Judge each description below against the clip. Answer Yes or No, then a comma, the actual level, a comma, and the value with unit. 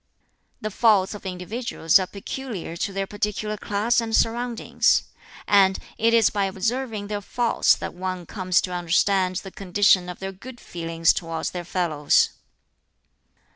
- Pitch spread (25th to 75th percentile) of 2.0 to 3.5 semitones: Yes, average, 3.2 semitones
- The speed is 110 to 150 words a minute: Yes, average, 145 wpm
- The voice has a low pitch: No, high, 195 Hz